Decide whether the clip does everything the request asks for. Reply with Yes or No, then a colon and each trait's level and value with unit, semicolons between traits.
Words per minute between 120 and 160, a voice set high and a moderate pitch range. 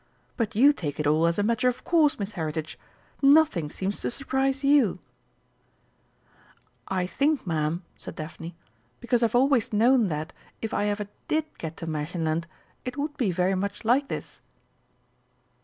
No: average, 155 wpm; high, 205 Hz; wide, 8.1 semitones